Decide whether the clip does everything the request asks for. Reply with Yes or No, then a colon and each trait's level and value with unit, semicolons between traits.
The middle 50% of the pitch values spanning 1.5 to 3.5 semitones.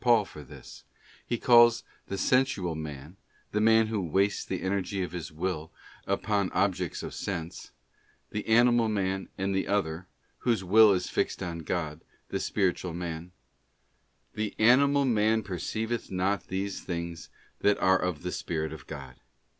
No: average, 4.1 semitones